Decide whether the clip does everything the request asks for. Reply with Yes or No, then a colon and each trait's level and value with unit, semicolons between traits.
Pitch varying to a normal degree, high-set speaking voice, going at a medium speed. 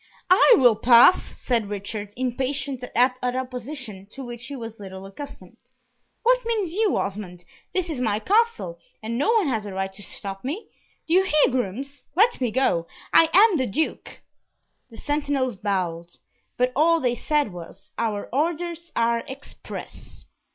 No: wide, 6.8 semitones; very high, 250 Hz; average, 160 wpm